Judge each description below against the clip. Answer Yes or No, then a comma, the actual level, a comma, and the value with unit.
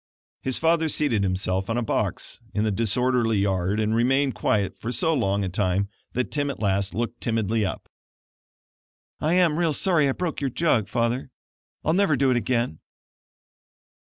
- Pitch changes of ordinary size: No, wide, 5.8 semitones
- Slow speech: No, average, 170 wpm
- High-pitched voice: No, low, 115 Hz